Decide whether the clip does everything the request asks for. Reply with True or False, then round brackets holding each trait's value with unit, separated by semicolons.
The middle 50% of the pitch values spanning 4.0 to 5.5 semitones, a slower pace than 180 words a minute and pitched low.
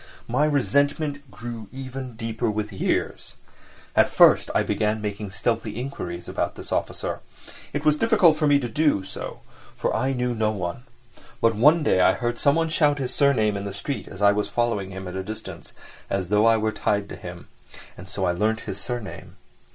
False (5.2 semitones; 190 wpm; 115 Hz)